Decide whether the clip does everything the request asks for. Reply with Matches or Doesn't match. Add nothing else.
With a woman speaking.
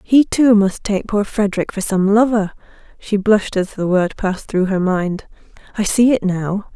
Matches